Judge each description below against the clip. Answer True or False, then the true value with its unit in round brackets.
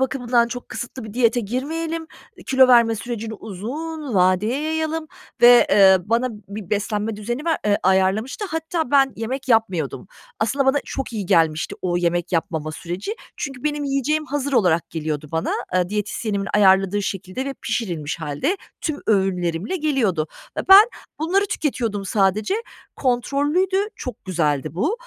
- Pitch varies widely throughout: True (6.6 semitones)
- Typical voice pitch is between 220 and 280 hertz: True (225 Hz)